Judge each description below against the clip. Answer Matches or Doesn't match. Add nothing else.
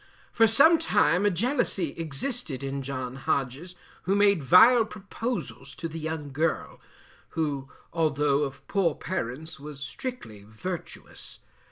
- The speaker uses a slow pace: Matches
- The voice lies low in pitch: Doesn't match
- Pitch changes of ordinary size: Doesn't match